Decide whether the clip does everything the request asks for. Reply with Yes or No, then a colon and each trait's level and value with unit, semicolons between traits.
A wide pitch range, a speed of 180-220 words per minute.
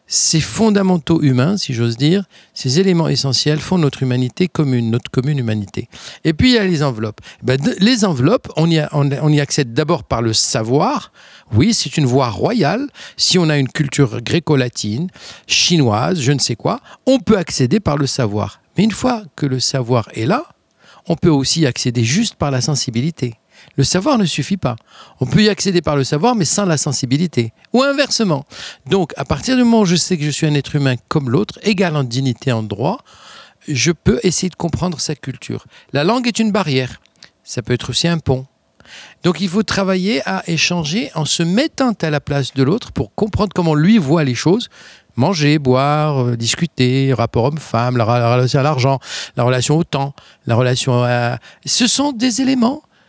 Yes: wide, 6.1 semitones; average, 190 wpm